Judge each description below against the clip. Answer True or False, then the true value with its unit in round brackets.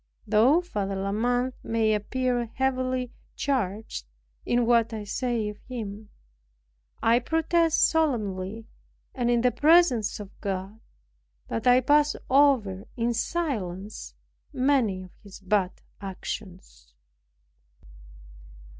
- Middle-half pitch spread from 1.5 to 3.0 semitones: False (4.3 semitones)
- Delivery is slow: True (110 wpm)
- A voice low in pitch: False (230 Hz)